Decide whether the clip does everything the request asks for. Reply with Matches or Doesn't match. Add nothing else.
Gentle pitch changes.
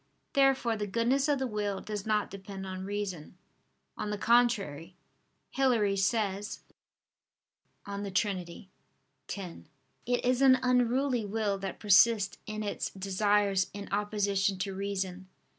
Doesn't match